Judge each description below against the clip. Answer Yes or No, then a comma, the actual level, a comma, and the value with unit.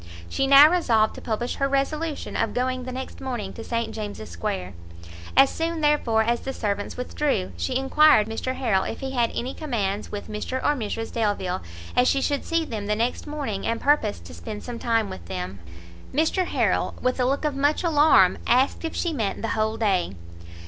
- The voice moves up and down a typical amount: Yes, average, 4.8 semitones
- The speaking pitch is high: Yes, high, 240 Hz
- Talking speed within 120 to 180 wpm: No, average, 200 wpm